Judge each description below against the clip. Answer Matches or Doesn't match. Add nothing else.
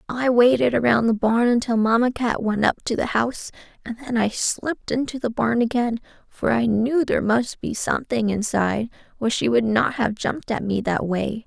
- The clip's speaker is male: Doesn't match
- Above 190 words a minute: Matches